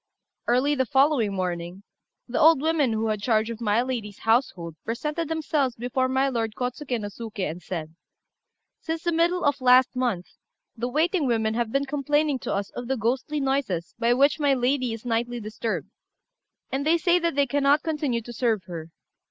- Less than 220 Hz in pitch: No, very high, 250 Hz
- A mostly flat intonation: No, average, 4.4 semitones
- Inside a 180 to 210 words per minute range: Yes, average, 185 wpm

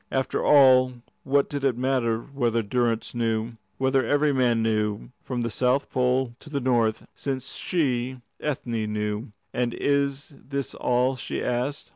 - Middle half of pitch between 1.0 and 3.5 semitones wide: Yes, narrow, 2.6 semitones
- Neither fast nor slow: Yes, average, 150 wpm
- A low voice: Yes, low, 125 Hz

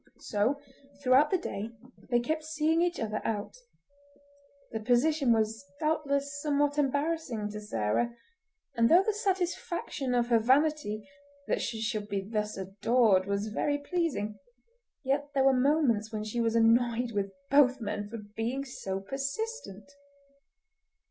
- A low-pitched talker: No, high, 240 Hz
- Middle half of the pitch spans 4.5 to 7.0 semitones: Yes, average, 5.2 semitones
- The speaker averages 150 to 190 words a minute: No, average, 140 wpm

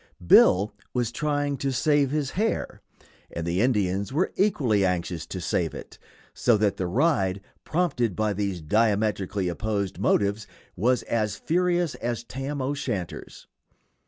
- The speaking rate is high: No, slow, 135 wpm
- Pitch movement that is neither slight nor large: No, wide, 6.3 semitones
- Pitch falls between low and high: No, low, 110 Hz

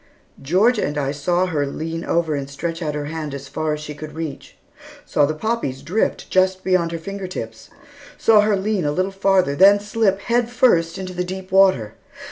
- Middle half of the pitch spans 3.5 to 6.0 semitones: Yes, average, 4.5 semitones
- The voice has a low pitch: No, medium, 170 Hz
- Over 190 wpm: Yes, average, 200 wpm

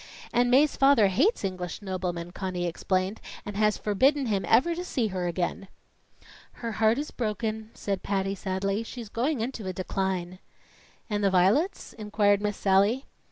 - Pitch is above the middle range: Yes, high, 205 Hz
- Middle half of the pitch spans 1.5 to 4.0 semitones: Yes, average, 3.7 semitones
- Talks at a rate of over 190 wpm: No, average, 160 wpm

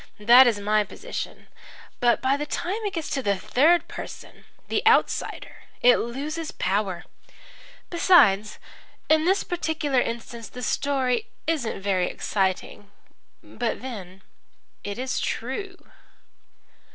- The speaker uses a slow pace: Yes, slow, 115 wpm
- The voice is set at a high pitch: Yes, very high, 250 Hz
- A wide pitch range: Yes, wide, 7.0 semitones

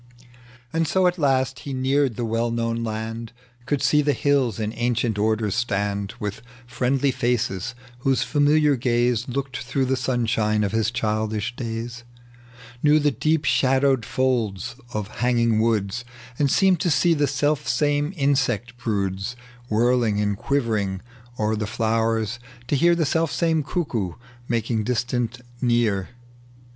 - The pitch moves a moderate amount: Yes, average, 3.9 semitones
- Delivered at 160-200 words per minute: No, average, 140 wpm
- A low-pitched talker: Yes, low, 120 Hz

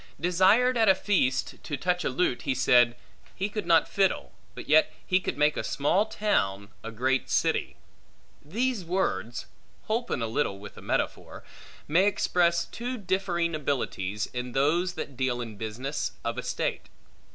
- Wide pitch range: Yes, wide, 7.4 semitones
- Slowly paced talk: No, average, 160 wpm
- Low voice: No, medium, 155 Hz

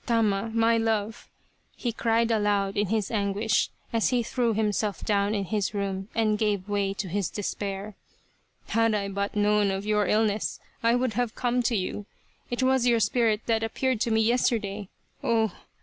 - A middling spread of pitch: No, narrow, 2.2 semitones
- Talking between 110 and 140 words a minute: No, average, 180 wpm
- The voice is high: Yes, high, 215 Hz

